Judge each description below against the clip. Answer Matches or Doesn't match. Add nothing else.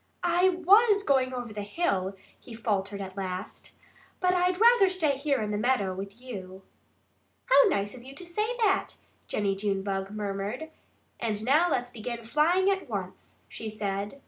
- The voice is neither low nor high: Doesn't match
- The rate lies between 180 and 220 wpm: Doesn't match